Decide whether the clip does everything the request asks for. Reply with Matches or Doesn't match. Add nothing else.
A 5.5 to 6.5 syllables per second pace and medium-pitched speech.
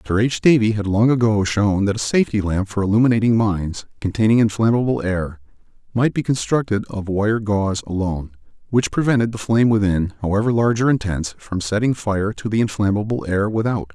Doesn't match